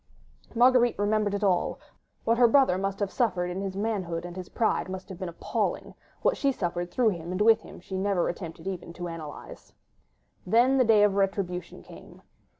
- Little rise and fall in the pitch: No, average, 3.9 semitones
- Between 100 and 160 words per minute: No, average, 190 wpm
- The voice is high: Yes, high, 195 Hz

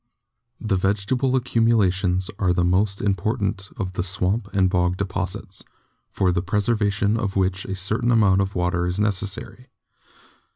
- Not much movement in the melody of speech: Yes, narrow, 2.3 semitones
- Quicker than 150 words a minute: No, average, 140 wpm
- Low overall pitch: Yes, very low, 95 Hz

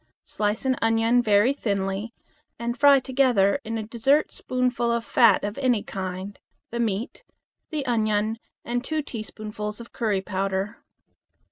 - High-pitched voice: Yes, high, 225 Hz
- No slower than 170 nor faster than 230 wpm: No, slow, 135 wpm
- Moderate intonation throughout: Yes, average, 3.0 semitones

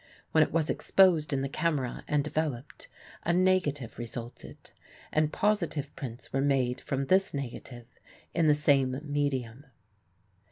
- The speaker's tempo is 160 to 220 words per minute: No, slow, 135 wpm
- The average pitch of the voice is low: No, medium, 145 Hz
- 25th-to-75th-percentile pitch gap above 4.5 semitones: No, average, 3.1 semitones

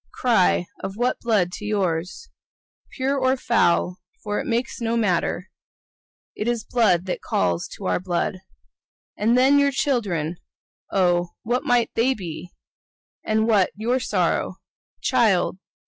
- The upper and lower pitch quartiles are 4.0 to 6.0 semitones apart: Yes, average, 5.1 semitones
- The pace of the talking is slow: Yes, slow, 130 wpm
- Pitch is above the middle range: Yes, high, 215 Hz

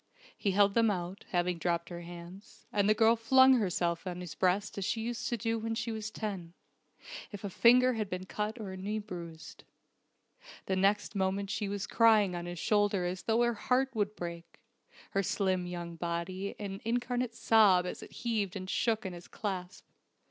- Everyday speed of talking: Yes, average, 190 wpm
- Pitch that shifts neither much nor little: Yes, average, 3.7 semitones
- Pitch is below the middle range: No, high, 200 Hz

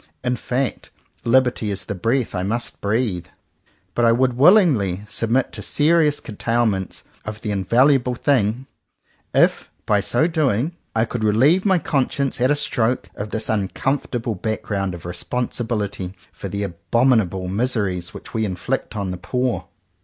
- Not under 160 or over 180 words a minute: No, average, 145 wpm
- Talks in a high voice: No, low, 115 Hz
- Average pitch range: Yes, average, 4.4 semitones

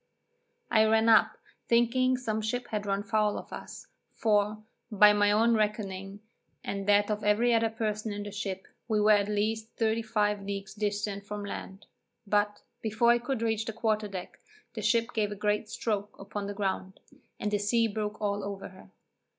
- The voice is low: No, high, 210 Hz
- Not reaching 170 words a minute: No, average, 180 wpm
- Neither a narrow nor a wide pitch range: No, narrow, 1.4 semitones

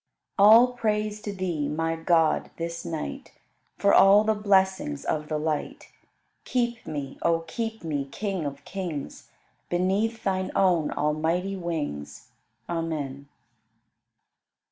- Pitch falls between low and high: Yes, medium, 170 Hz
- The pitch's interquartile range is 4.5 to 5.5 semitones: Yes, average, 4.9 semitones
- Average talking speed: No, slow, 120 wpm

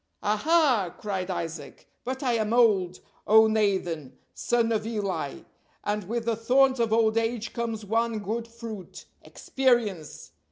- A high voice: Yes, high, 220 Hz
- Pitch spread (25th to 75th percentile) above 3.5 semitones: No, narrow, 2.6 semitones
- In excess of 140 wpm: No, slow, 135 wpm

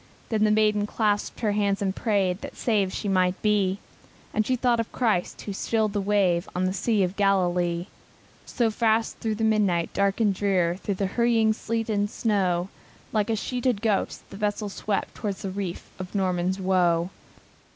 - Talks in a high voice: Yes, high, 205 Hz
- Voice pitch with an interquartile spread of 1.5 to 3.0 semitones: Yes, narrow, 2.6 semitones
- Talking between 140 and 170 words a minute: No, average, 180 wpm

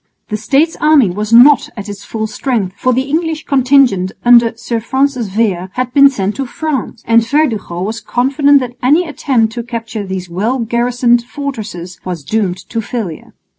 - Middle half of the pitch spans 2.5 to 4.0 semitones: No, average, 4.4 semitones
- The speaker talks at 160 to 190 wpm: Yes, average, 170 wpm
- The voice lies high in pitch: Yes, high, 235 Hz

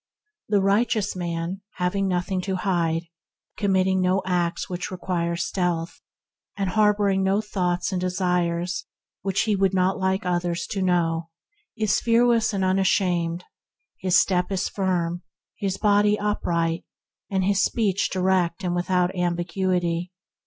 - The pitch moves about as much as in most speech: No, narrow, 1.9 semitones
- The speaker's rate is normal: No, slow, 130 wpm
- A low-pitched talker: No, medium, 185 Hz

